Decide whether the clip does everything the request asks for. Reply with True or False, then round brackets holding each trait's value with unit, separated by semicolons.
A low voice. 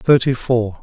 True (120 Hz)